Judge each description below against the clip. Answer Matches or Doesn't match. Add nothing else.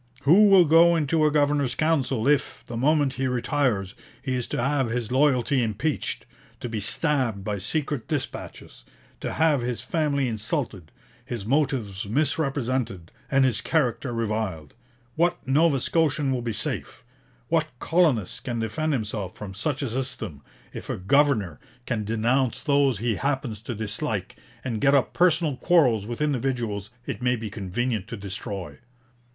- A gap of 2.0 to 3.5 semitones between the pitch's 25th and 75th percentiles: Doesn't match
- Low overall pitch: Matches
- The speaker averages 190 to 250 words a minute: Doesn't match